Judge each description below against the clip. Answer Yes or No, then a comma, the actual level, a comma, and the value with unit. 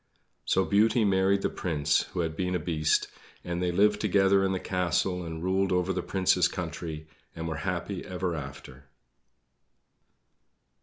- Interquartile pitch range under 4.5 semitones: Yes, average, 2.7 semitones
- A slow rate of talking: No, average, 155 wpm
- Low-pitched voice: Yes, very low, 90 Hz